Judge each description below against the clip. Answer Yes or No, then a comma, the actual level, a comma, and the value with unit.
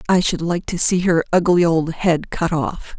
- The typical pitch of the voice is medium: Yes, medium, 170 Hz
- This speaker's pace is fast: Yes, fast, 220 wpm